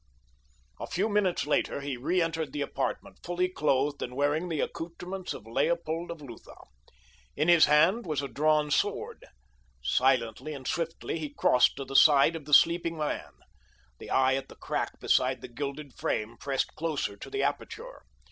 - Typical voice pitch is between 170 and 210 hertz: No, medium, 150 Hz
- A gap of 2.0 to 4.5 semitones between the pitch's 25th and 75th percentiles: Yes, average, 3.7 semitones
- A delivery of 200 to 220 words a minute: No, average, 165 wpm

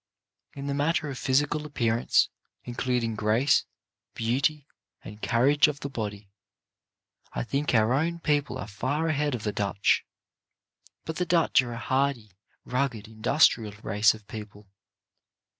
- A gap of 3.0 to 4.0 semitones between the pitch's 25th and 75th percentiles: No, average, 5.0 semitones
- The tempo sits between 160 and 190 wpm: No, average, 140 wpm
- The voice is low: Yes, low, 125 Hz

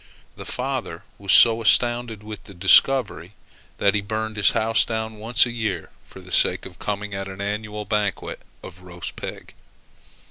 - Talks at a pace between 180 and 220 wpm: No, average, 170 wpm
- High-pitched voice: No, low, 105 Hz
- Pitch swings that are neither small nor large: No, narrow, 2.0 semitones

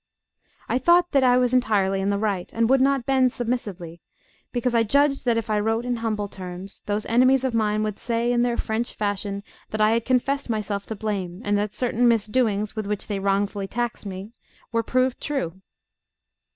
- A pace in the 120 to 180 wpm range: No, average, 195 wpm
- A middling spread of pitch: Yes, average, 3.4 semitones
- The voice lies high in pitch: Yes, high, 225 Hz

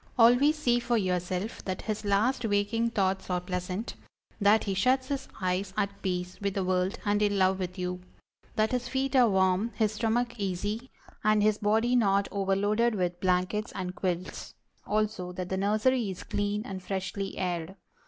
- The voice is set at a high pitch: Yes, high, 200 Hz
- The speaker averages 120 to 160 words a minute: No, average, 175 wpm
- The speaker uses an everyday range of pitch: Yes, average, 3.1 semitones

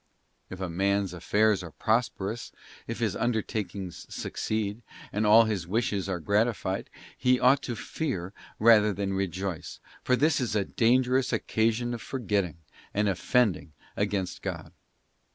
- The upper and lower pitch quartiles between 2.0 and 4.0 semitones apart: Yes, average, 3.6 semitones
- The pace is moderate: Yes, average, 145 wpm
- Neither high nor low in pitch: No, low, 105 Hz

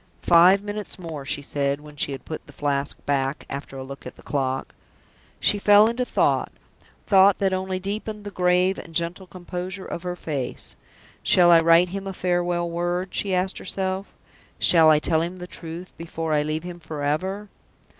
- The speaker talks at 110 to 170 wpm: No, average, 185 wpm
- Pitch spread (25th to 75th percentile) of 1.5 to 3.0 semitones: No, average, 3.5 semitones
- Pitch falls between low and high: Yes, medium, 175 Hz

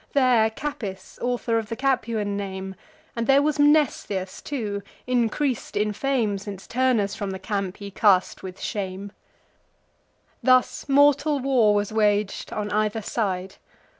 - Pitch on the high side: Yes, high, 215 Hz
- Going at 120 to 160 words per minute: Yes, slow, 135 wpm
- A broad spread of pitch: No, average, 4.3 semitones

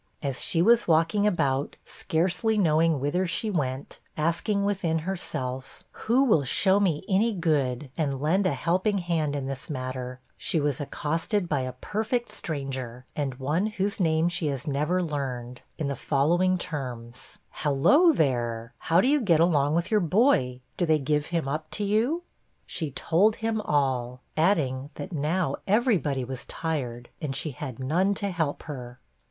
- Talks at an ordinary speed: Yes, average, 165 wpm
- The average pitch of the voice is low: No, medium, 155 Hz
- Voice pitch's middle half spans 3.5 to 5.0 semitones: No, wide, 5.6 semitones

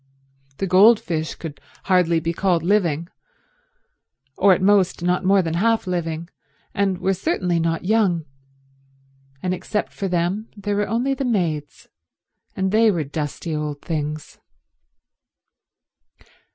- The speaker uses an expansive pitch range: No, average, 3.5 semitones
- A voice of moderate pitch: Yes, medium, 180 Hz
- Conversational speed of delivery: No, slow, 125 wpm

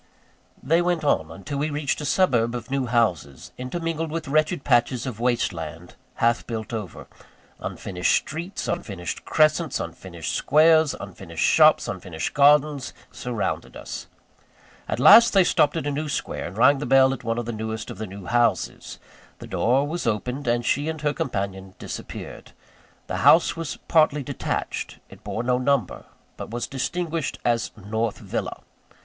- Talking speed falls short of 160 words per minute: No, average, 165 wpm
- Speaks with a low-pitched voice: Yes, low, 130 Hz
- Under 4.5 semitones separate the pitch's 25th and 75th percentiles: No, average, 5.2 semitones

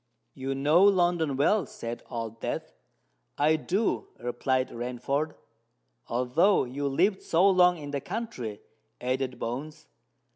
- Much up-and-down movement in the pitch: Yes, wide, 5.8 semitones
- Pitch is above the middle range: No, medium, 140 Hz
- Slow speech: Yes, slow, 120 wpm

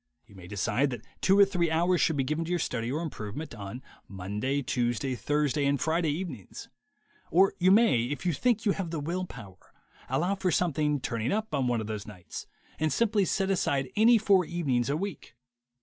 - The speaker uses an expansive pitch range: Yes, wide, 6.8 semitones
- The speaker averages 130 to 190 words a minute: No, average, 200 wpm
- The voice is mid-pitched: Yes, medium, 150 Hz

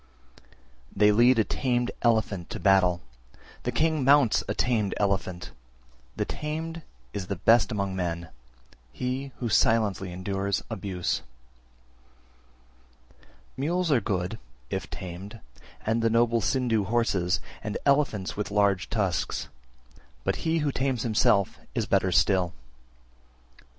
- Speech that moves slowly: Yes, slow, 125 wpm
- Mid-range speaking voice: No, low, 105 Hz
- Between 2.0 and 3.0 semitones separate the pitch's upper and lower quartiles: No, average, 4.5 semitones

